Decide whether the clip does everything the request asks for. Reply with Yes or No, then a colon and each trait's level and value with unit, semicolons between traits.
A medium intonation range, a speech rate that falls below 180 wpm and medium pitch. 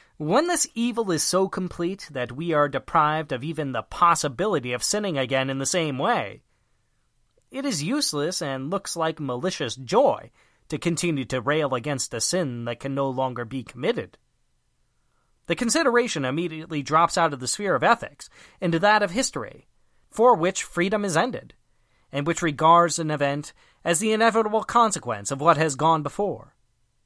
No: wide, 5.7 semitones; average, 165 wpm; medium, 160 Hz